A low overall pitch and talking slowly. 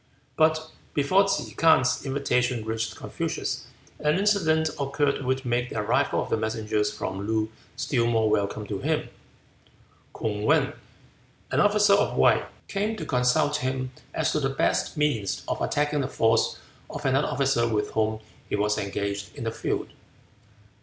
No: low, 130 Hz; average, 155 wpm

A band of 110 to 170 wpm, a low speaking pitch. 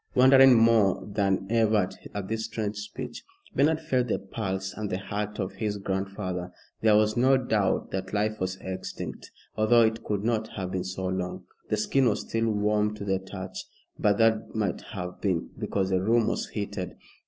No: average, 180 wpm; low, 105 Hz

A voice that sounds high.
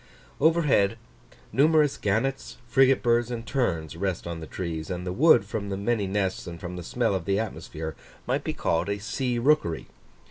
No: low, 100 Hz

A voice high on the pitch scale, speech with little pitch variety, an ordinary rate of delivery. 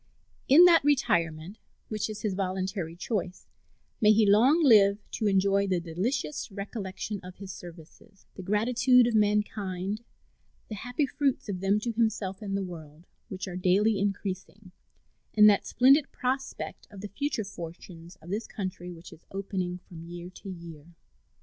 No: high, 200 Hz; average, 3.2 semitones; average, 155 wpm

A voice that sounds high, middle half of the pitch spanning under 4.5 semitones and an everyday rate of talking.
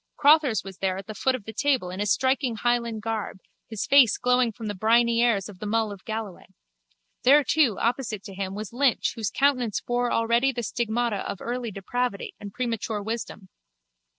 Yes: high, 230 Hz; average, 3.1 semitones; average, 190 wpm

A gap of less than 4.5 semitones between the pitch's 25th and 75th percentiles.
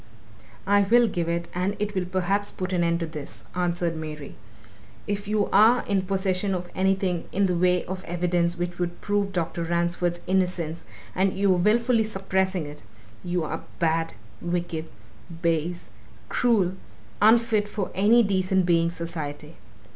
Yes: narrow, 2.6 semitones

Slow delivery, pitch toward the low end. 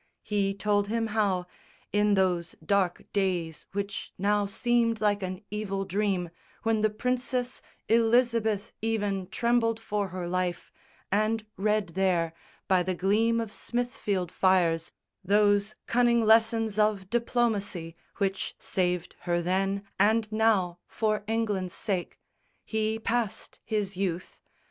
No: slow, 125 wpm; high, 205 Hz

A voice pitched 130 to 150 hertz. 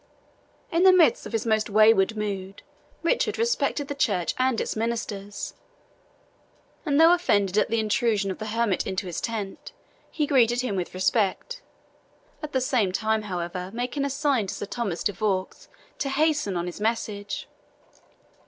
No: high, 220 Hz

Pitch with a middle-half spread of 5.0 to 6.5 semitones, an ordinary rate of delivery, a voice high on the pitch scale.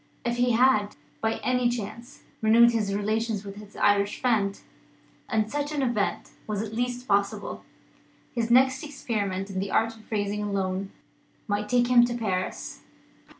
No: average, 3.0 semitones; average, 160 wpm; high, 220 Hz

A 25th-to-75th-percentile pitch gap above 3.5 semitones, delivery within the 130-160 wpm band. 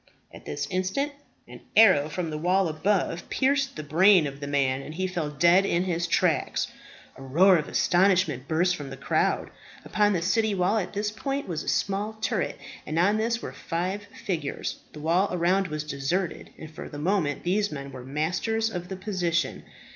No: average, 4.5 semitones; average, 190 wpm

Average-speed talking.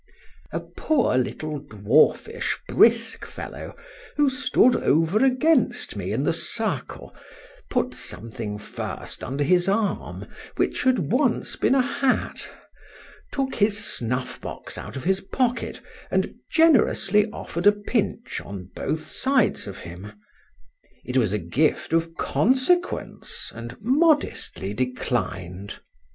No: slow, 120 wpm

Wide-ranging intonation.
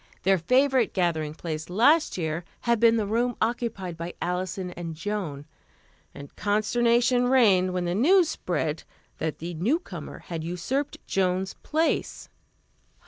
Yes: wide, 5.9 semitones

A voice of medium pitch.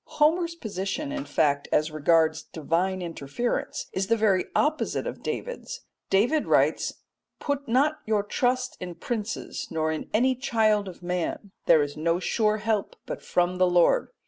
No: high, 205 Hz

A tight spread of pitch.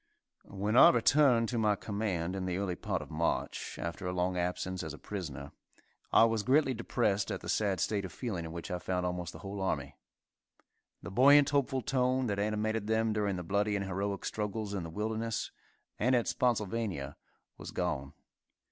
No: average, 3.9 semitones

